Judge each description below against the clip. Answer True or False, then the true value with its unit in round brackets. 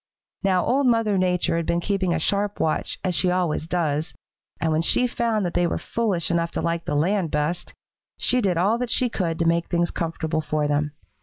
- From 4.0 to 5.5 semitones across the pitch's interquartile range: False (3.6 semitones)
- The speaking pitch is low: False (175 Hz)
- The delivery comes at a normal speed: False (215 wpm)